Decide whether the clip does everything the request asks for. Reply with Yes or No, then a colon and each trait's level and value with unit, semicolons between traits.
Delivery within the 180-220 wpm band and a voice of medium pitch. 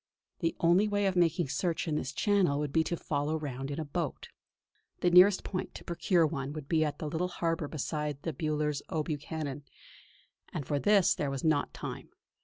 Yes: average, 195 wpm; medium, 155 Hz